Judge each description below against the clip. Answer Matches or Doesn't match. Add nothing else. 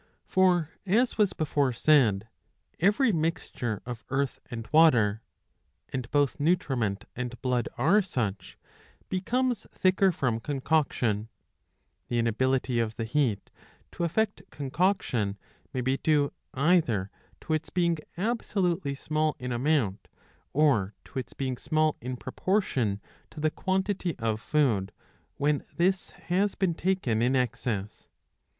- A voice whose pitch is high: Doesn't match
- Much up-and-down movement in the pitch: Matches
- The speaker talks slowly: Matches